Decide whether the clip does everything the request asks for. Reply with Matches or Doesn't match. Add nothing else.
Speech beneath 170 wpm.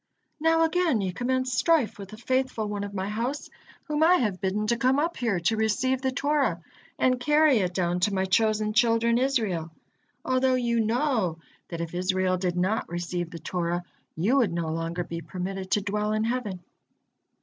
Doesn't match